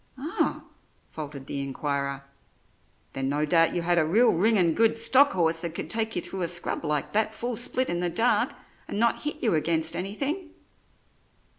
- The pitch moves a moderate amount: No, wide, 6.4 semitones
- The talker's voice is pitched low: No, medium, 175 Hz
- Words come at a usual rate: Yes, average, 180 wpm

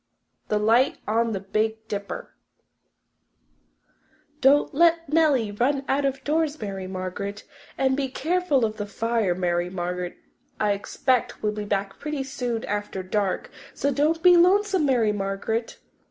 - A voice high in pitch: Yes, high, 225 Hz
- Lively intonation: Yes, wide, 5.8 semitones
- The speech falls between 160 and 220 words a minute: No, average, 140 wpm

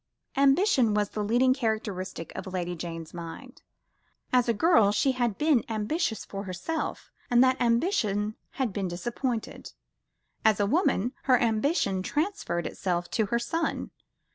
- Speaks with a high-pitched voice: Yes, high, 225 Hz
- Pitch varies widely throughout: No, average, 5.0 semitones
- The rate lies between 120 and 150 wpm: Yes, average, 140 wpm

